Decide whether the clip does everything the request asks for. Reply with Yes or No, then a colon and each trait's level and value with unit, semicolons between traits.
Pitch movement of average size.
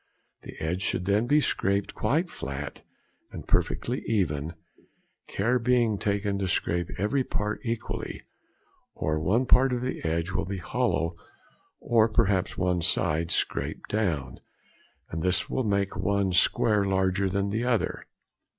Yes: average, 4.3 semitones